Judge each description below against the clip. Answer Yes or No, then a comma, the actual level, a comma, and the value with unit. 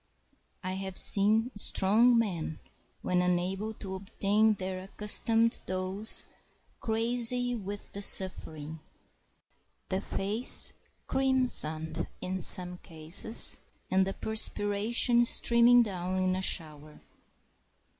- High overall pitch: Yes, high, 195 Hz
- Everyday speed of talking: No, slow, 100 wpm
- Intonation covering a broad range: No, average, 3.4 semitones